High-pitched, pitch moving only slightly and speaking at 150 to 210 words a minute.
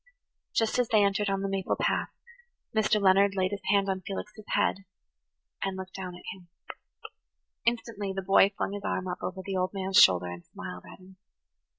Yes: high, 195 Hz; narrow, 1.4 semitones; average, 190 wpm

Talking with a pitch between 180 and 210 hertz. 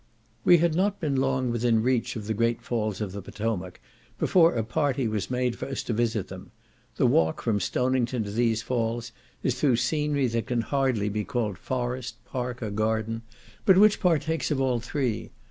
No: low, 120 Hz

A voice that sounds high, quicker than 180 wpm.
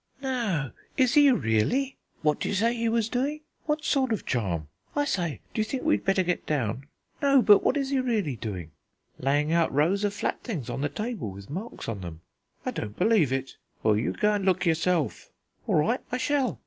Yes: high, 195 Hz; average, 200 wpm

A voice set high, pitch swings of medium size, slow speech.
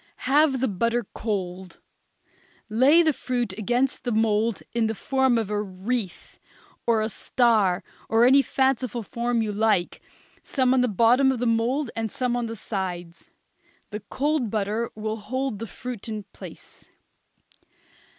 No: high, 230 Hz; average, 3.2 semitones; average, 150 wpm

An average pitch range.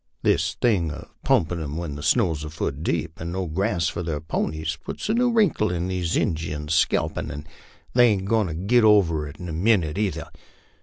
Yes: average, 4.5 semitones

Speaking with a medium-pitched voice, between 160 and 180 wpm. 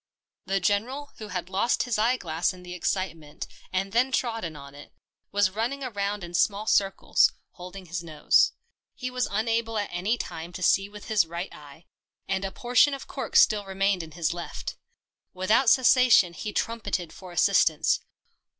No: high, 195 Hz; average, 170 wpm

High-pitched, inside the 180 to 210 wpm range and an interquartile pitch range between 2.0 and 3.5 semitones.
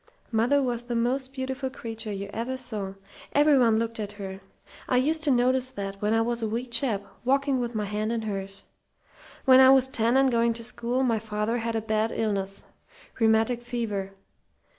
Yes: high, 230 Hz; average, 185 wpm; average, 3.1 semitones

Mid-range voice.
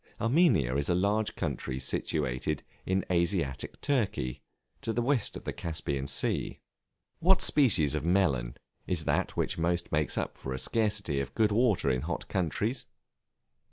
No: very low, 85 Hz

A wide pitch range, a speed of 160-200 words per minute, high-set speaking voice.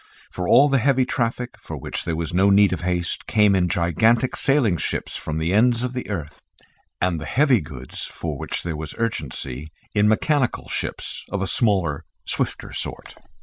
No: wide, 6.4 semitones; average, 185 wpm; low, 100 Hz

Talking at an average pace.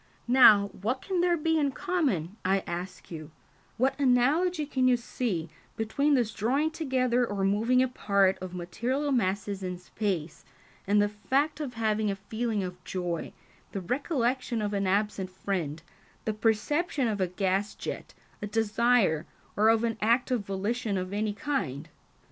Yes: average, 160 wpm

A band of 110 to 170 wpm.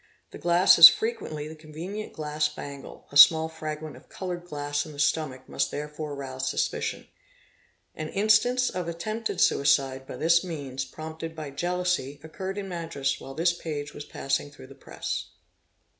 Yes: average, 160 wpm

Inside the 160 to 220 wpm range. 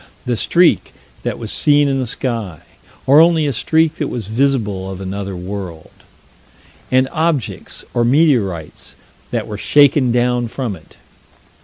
No: average, 145 wpm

